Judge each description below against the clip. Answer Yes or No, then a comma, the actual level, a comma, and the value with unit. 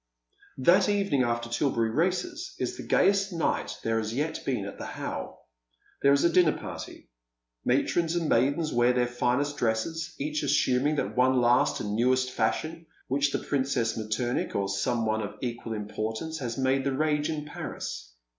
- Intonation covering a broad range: No, average, 4.7 semitones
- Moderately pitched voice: No, low, 130 Hz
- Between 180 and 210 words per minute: No, average, 170 wpm